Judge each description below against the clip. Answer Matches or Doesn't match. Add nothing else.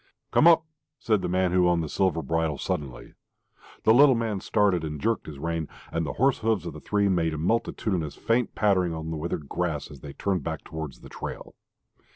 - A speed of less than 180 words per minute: Doesn't match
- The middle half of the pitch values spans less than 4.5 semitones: Doesn't match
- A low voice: Matches